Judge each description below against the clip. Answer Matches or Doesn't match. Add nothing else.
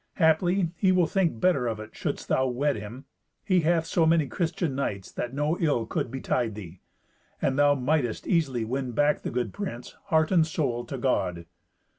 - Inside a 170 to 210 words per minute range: Matches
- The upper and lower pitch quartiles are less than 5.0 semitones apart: Doesn't match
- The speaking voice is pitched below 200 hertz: Matches